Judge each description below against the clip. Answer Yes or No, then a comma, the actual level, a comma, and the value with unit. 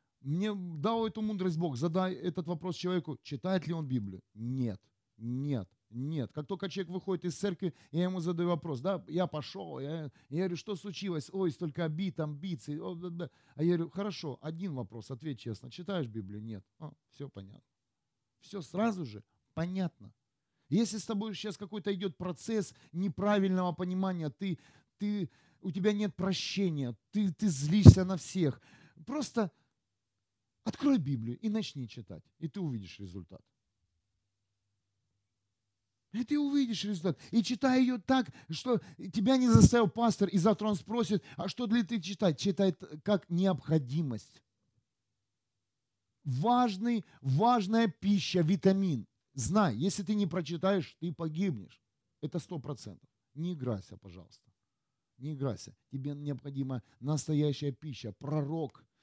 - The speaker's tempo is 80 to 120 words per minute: No, average, 140 wpm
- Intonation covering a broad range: Yes, wide, 7.4 semitones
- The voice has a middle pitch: Yes, medium, 165 Hz